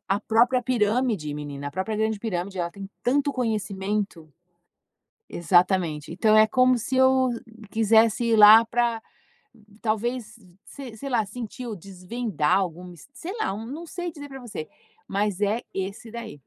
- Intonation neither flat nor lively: Yes, average, 4.4 semitones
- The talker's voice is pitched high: Yes, high, 215 Hz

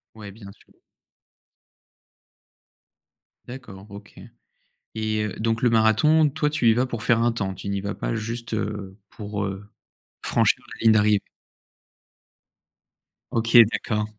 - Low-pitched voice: Yes, low, 110 Hz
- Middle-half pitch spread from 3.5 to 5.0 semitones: No, narrow, 2.4 semitones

